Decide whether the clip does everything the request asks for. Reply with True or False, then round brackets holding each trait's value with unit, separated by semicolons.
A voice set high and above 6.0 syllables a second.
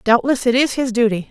False (240 Hz; 5.8 syllables/s)